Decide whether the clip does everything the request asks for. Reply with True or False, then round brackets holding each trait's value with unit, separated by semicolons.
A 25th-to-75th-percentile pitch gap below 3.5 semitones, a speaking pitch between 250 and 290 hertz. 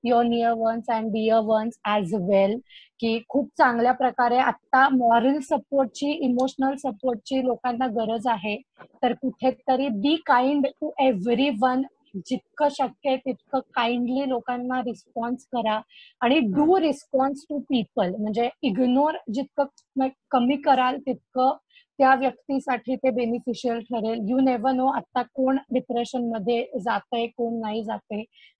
True (2.4 semitones; 255 Hz)